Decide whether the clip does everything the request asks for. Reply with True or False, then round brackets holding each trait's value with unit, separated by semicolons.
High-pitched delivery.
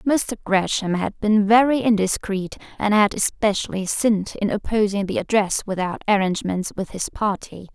True (205 Hz)